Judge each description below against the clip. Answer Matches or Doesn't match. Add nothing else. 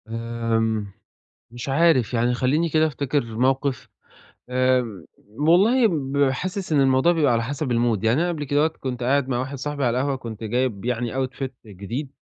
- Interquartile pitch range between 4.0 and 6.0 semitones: Doesn't match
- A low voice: Matches